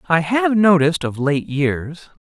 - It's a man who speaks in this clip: Yes, male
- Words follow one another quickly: No, average, 160 wpm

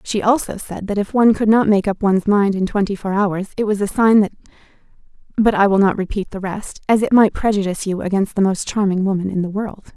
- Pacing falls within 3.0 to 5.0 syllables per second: No, 6.0 syllables/s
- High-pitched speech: Yes, high, 200 Hz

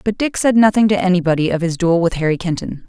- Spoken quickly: Yes, fast, 250 wpm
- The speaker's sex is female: Yes, female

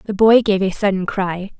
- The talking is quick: Yes, fast, 225 wpm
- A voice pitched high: Yes, high, 200 Hz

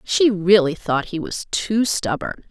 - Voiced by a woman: Yes, female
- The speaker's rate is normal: Yes, average, 170 wpm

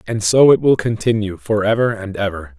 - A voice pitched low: Yes, low, 110 Hz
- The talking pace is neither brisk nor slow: No, fast, 210 wpm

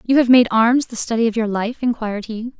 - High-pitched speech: Yes, high, 230 Hz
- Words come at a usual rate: No, fast, 255 wpm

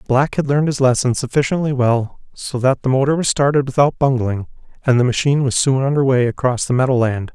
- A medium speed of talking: No, fast, 215 wpm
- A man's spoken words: Yes, male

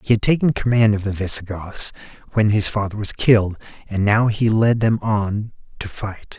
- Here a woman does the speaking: No, male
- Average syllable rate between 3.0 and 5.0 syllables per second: Yes, 4.9 syllables/s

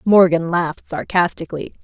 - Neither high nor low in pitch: Yes, medium, 175 Hz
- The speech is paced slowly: Yes, slow, 100 wpm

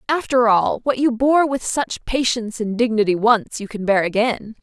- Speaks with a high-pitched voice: Yes, high, 235 Hz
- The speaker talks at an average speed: Yes, average, 195 wpm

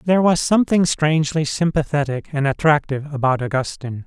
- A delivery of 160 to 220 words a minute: No, slow, 135 wpm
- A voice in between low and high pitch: Yes, medium, 150 Hz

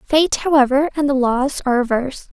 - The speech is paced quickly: No, average, 175 wpm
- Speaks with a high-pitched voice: Yes, very high, 270 Hz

